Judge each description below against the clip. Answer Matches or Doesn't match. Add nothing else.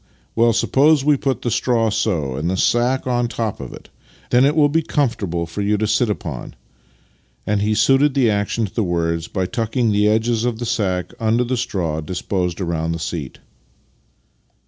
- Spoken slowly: Doesn't match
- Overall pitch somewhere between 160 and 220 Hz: Doesn't match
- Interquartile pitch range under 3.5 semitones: Doesn't match